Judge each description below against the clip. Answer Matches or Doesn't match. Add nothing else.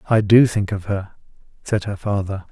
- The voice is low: Matches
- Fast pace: Doesn't match